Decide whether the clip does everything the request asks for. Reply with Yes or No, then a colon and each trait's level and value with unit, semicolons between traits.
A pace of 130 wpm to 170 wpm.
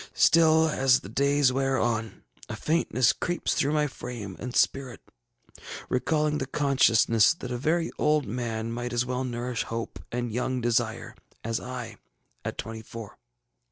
Yes: average, 155 wpm